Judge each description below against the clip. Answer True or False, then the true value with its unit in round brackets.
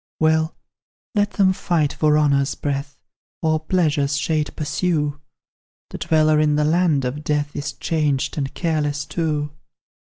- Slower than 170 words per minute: True (135 wpm)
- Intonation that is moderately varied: False (1.6 semitones)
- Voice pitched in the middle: True (150 Hz)